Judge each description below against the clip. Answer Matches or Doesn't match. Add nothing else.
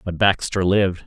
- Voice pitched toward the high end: Doesn't match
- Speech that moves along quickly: Doesn't match